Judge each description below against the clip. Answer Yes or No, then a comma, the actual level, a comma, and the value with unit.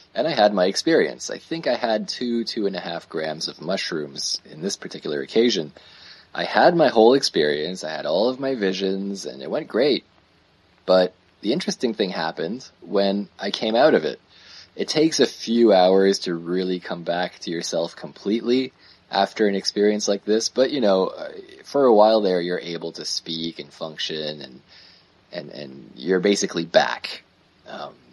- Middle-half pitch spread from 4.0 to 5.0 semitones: No, average, 3.3 semitones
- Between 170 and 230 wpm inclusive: Yes, average, 180 wpm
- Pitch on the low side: Yes, very low, 95 Hz